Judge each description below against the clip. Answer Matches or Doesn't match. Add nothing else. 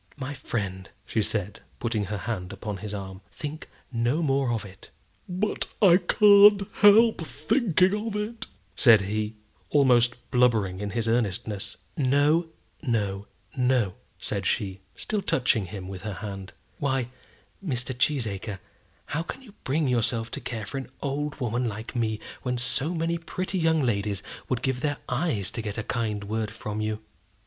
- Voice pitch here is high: Doesn't match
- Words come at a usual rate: Matches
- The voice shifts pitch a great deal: Matches